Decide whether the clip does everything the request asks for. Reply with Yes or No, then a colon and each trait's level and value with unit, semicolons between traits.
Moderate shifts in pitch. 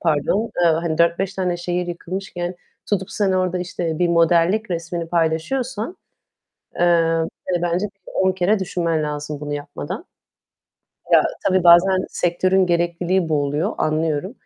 No: narrow, 2.3 semitones